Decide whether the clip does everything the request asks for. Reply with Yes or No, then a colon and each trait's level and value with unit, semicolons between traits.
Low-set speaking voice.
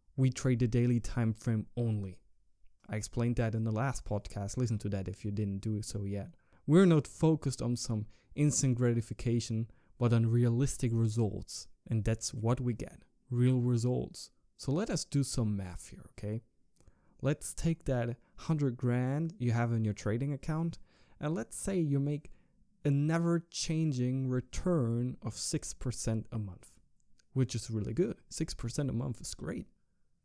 Yes: low, 120 Hz